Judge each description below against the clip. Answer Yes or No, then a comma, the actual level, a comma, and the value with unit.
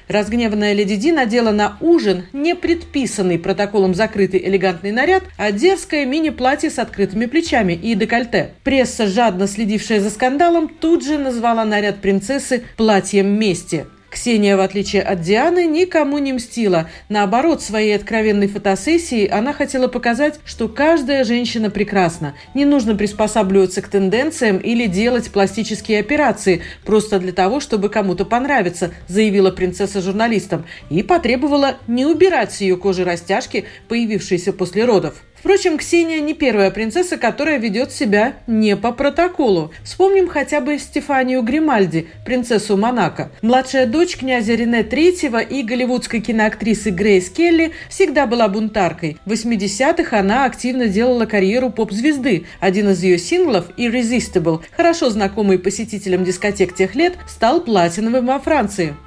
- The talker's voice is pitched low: No, high, 225 Hz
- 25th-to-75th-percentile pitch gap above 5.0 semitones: Yes, wide, 5.4 semitones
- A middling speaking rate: Yes, average, 135 wpm